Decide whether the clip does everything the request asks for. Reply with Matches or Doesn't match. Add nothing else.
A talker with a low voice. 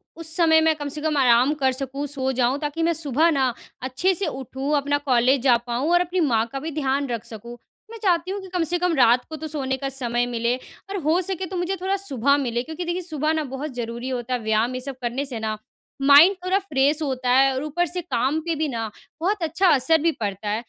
Doesn't match